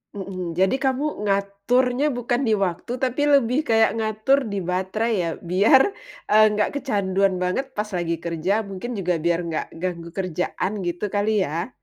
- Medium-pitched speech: No, high, 200 Hz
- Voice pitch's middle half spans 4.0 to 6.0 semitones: Yes, average, 4.7 semitones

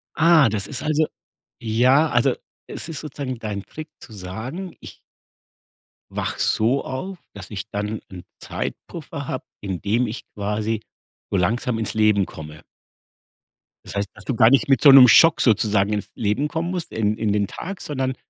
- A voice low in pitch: Yes, low, 115 Hz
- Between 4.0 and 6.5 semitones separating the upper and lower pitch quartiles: Yes, average, 5.3 semitones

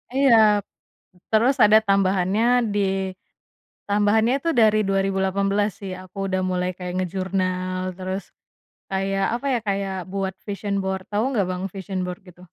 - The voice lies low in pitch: No, high, 195 Hz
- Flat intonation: Yes, narrow, 1.8 semitones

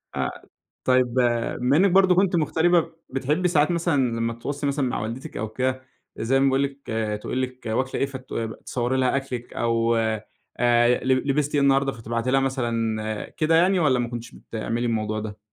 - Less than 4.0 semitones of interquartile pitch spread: Yes, average, 3.6 semitones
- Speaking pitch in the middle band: No, low, 130 Hz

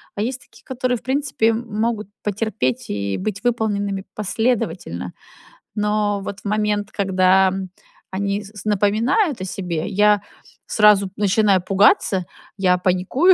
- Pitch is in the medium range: No, high, 205 Hz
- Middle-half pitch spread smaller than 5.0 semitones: Yes, narrow, 2.6 semitones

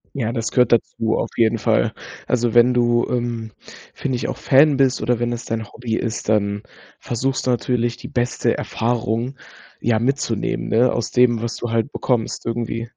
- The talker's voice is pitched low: Yes, low, 120 Hz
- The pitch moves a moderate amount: No, narrow, 1.6 semitones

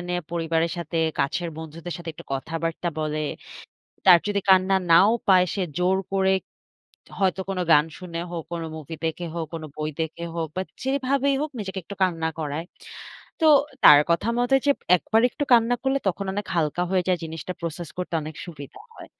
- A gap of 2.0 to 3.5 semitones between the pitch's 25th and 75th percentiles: Yes, average, 2.9 semitones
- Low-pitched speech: No, medium, 175 Hz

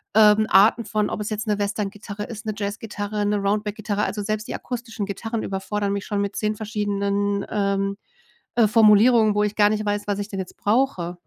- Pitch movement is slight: Yes, narrow, 1.2 semitones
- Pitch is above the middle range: Yes, high, 210 Hz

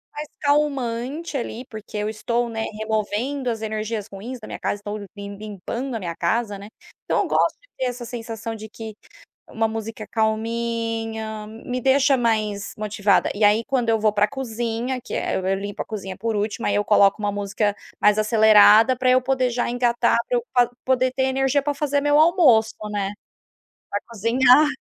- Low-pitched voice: No, high, 225 Hz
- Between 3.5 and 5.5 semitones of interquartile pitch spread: No, average, 3.1 semitones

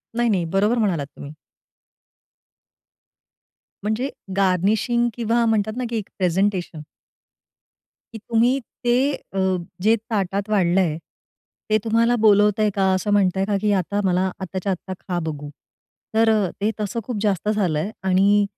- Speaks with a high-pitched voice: Yes, high, 205 Hz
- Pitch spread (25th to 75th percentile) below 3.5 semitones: Yes, average, 2.7 semitones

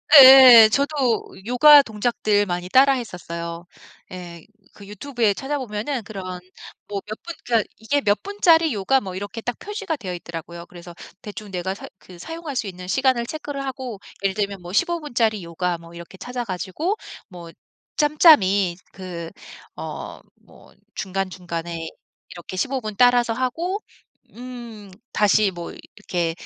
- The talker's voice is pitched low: No, high, 210 Hz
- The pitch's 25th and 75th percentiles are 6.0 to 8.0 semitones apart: Yes, wide, 6.3 semitones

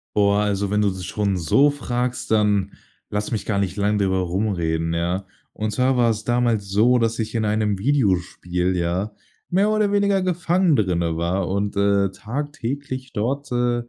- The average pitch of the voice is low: Yes, low, 105 Hz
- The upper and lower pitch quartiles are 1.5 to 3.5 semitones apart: No, average, 4.5 semitones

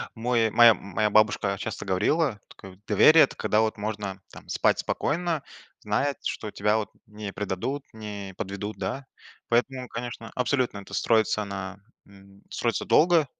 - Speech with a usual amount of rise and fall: Yes, average, 3.8 semitones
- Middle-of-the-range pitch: No, low, 110 Hz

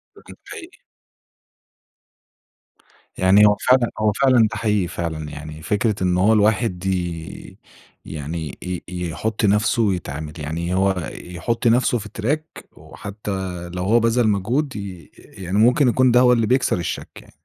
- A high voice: No, low, 105 Hz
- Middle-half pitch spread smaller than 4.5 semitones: No, average, 4.8 semitones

